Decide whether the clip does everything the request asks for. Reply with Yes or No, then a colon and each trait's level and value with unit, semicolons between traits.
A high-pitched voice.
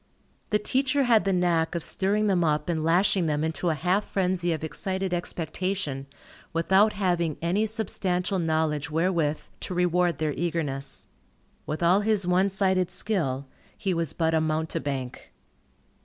No: medium, 175 Hz